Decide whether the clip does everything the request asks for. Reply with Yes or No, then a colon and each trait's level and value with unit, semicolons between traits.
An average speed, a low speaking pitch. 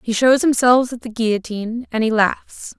No: average, 195 wpm; high, 230 Hz